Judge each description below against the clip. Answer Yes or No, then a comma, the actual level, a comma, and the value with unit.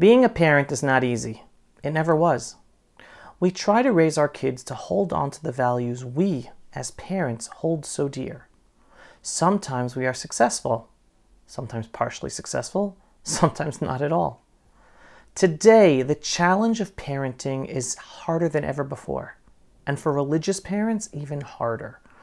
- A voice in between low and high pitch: Yes, medium, 145 Hz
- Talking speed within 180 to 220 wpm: No, average, 145 wpm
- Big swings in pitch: Yes, wide, 5.8 semitones